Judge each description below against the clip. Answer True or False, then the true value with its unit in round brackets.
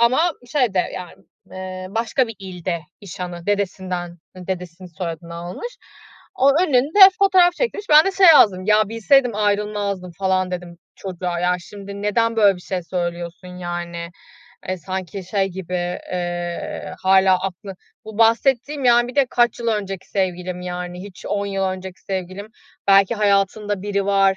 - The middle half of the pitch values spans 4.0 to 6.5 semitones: False (3.3 semitones)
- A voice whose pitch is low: False (195 Hz)